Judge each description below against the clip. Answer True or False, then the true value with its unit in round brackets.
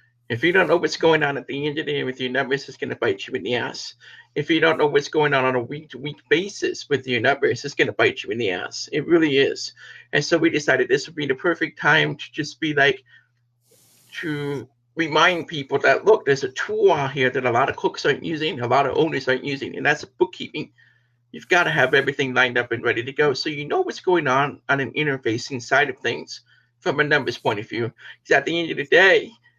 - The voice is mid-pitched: True (150 Hz)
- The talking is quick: True (260 wpm)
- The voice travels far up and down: True (6.2 semitones)